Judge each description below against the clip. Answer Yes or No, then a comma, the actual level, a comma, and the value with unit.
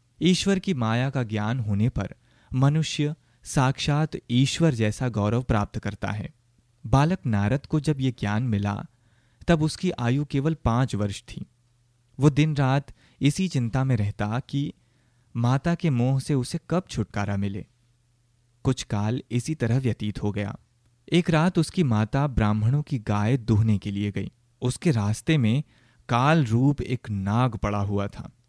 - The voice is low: Yes, low, 120 Hz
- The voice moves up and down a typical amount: Yes, average, 4.4 semitones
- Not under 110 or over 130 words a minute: No, average, 155 wpm